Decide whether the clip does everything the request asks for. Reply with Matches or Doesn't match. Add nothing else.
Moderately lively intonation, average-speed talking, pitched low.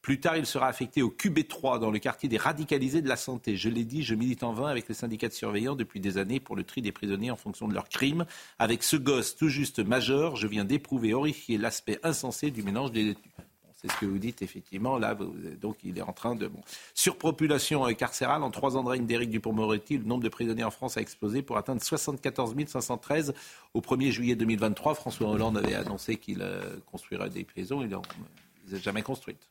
Doesn't match